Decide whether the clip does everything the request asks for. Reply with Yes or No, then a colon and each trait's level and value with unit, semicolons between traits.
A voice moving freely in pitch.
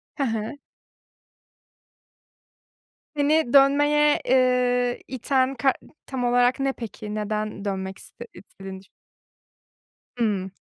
No: average, 4.2 semitones